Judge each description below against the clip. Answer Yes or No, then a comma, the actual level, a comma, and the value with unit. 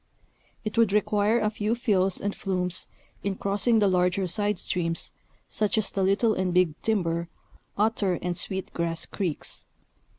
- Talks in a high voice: Yes, high, 195 Hz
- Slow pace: No, average, 155 wpm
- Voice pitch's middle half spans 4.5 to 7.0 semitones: No, average, 2.8 semitones